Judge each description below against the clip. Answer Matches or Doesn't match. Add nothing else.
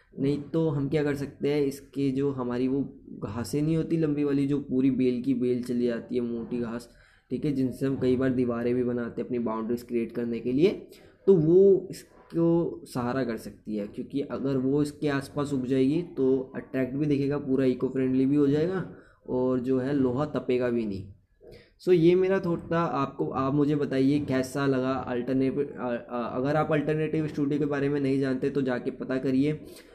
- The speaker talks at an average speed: Doesn't match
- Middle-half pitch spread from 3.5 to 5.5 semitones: Doesn't match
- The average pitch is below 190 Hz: Matches